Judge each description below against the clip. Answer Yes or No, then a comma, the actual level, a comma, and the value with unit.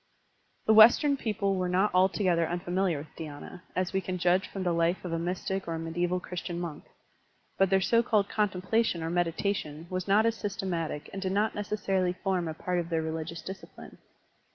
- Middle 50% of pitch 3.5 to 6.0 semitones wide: No, narrow, 2.6 semitones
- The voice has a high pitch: No, medium, 180 Hz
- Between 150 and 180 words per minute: No, average, 195 wpm